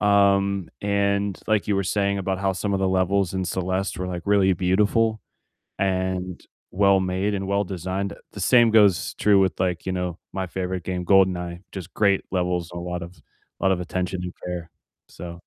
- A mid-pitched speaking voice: No, very low, 95 Hz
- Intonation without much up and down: Yes, narrow, 1.7 semitones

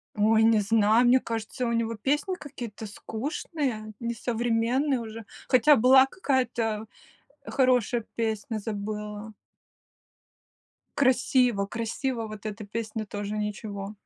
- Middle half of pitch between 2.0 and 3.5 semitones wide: Yes, average, 2.8 semitones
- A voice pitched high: Yes, high, 225 Hz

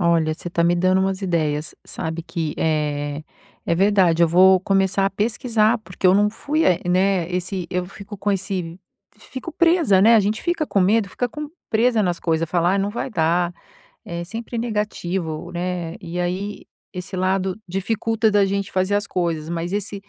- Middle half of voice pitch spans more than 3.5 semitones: No, average, 3.2 semitones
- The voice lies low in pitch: No, medium, 185 Hz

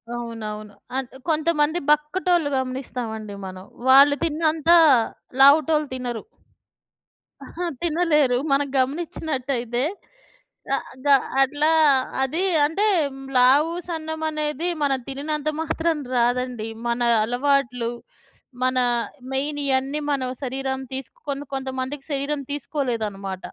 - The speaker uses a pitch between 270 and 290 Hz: Yes, very high, 275 Hz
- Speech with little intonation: No, average, 3.3 semitones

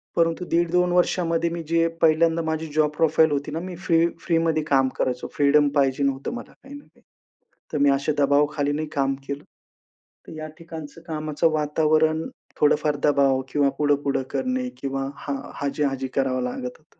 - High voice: No, medium, 150 Hz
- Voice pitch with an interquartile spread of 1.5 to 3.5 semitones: Yes, average, 2.8 semitones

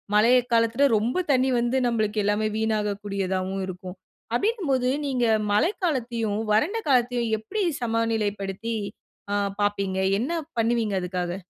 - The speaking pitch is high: Yes, high, 225 Hz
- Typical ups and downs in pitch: Yes, average, 3.3 semitones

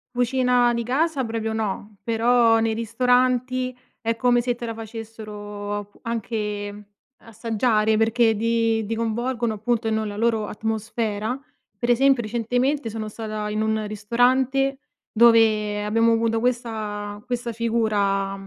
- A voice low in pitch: No, high, 225 Hz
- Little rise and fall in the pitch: Yes, narrow, 2.1 semitones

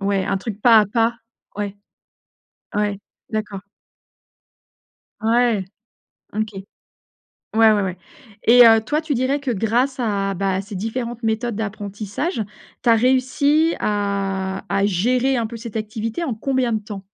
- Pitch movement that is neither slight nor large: Yes, average, 3.2 semitones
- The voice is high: Yes, high, 220 Hz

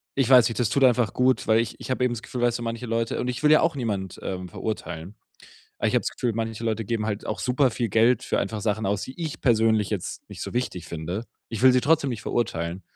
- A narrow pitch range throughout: No, average, 3.0 semitones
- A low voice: Yes, low, 115 Hz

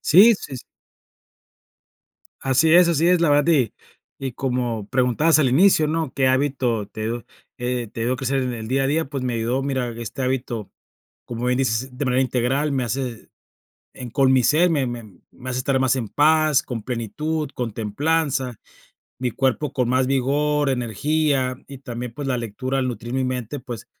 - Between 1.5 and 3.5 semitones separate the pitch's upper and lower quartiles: Yes, average, 2.9 semitones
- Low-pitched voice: Yes, low, 130 Hz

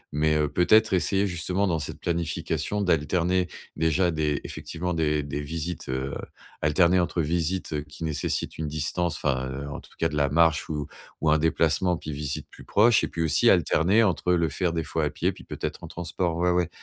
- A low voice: Yes, very low, 80 Hz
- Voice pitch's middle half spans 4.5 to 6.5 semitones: No, average, 3.0 semitones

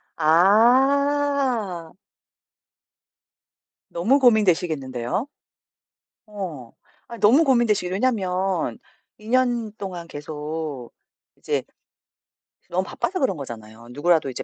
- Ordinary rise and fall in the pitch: No, wide, 7.3 semitones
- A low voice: No, high, 190 Hz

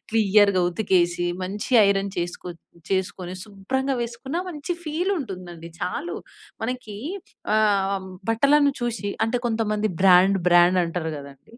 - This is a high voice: Yes, high, 200 Hz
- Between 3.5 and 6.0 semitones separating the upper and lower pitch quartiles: Yes, average, 5.0 semitones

